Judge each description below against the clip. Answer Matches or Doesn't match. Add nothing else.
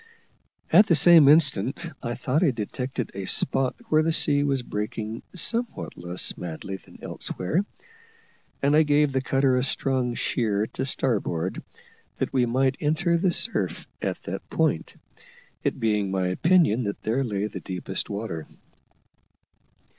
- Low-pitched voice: Matches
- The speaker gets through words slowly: Doesn't match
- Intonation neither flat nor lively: Doesn't match